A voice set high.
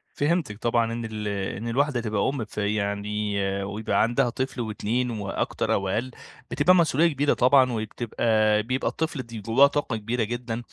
No: low, 115 Hz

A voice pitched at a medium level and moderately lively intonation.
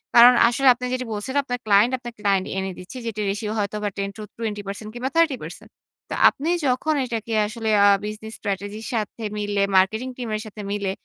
No: high, 215 Hz; average, 3.1 semitones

